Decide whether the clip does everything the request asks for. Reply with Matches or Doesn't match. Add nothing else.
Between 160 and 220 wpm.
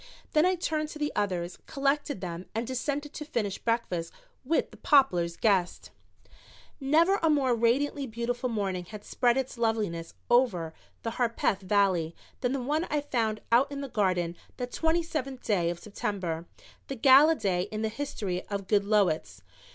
Matches